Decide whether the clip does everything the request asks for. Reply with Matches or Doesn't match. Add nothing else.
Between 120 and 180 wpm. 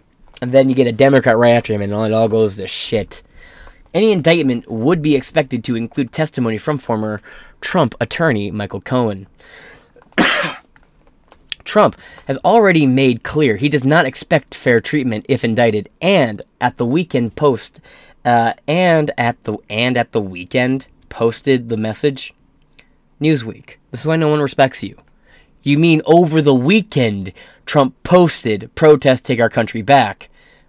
Matches